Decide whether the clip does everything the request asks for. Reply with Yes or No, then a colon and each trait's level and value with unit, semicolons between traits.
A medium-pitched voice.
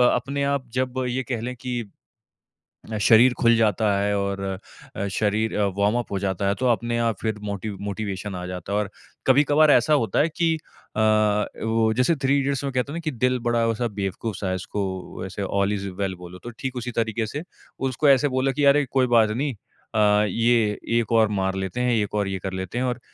No: low, 115 Hz